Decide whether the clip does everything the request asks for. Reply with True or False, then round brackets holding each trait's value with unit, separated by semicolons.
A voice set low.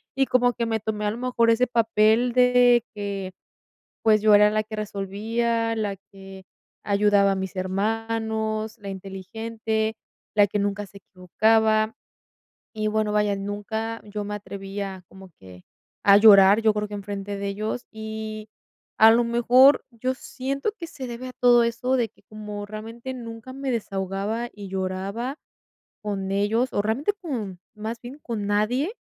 False (215 Hz)